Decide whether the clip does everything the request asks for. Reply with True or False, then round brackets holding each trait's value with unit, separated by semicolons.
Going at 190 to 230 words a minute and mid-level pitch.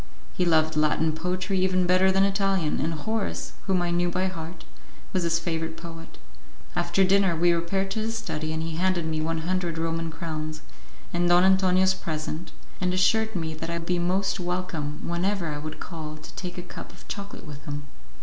True (195 wpm; 175 Hz)